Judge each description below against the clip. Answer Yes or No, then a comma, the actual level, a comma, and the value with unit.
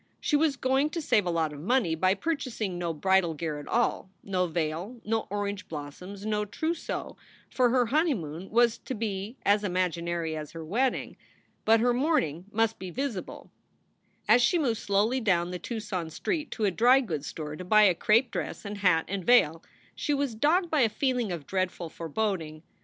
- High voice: Yes, high, 205 Hz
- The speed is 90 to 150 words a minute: No, average, 190 wpm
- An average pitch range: No, wide, 6.1 semitones